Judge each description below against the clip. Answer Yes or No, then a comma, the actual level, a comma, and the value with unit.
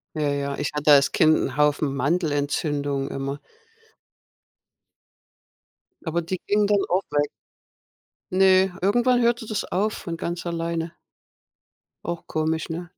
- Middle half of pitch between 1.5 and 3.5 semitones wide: No, average, 4.3 semitones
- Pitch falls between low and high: Yes, medium, 165 Hz